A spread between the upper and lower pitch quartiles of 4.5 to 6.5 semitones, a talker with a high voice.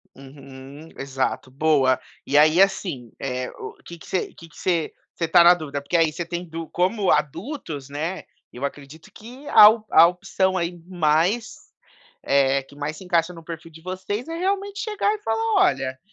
No: average, 5.0 semitones; medium, 165 Hz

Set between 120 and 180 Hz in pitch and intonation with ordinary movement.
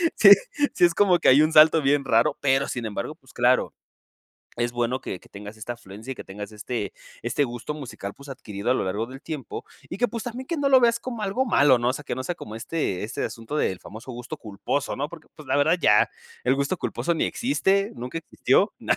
No: low, 135 Hz; wide, 6.2 semitones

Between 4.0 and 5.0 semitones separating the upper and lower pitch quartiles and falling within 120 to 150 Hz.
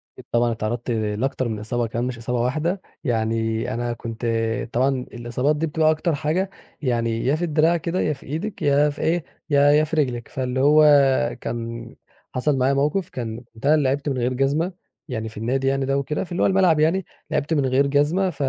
Yes: average, 4.5 semitones; low, 135 Hz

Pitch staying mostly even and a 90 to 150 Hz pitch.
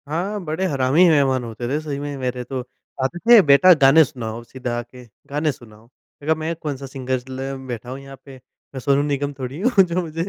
No: average, 3.4 semitones; medium, 140 Hz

